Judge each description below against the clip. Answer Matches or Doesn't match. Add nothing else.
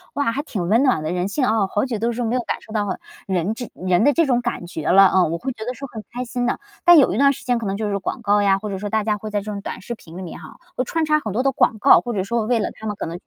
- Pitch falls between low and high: Doesn't match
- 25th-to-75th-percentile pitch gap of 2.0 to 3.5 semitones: Doesn't match